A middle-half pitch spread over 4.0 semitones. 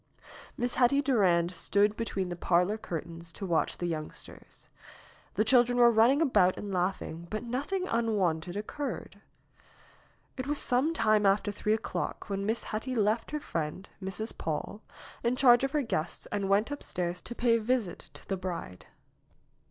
Yes: average, 5.2 semitones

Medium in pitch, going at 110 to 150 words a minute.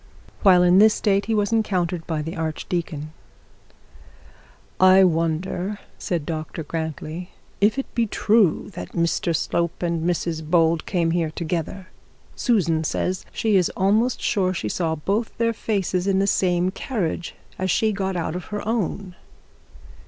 Yes: medium, 180 Hz; average, 145 wpm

